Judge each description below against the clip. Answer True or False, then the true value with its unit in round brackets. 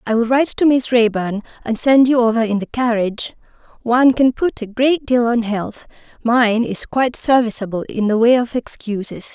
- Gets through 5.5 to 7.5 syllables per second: False (5.1 syllables/s)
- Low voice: False (235 Hz)